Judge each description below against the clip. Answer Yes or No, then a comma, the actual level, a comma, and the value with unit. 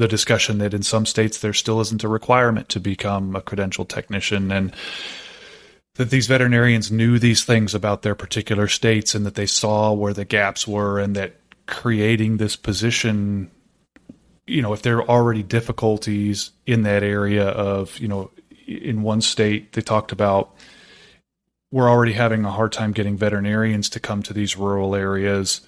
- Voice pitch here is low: Yes, low, 105 Hz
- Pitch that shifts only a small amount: Yes, narrow, 1.8 semitones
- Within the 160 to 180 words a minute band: Yes, average, 170 wpm